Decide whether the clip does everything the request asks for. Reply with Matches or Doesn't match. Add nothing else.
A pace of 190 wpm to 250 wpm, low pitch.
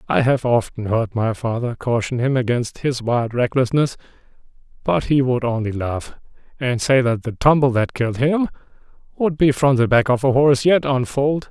Doesn't match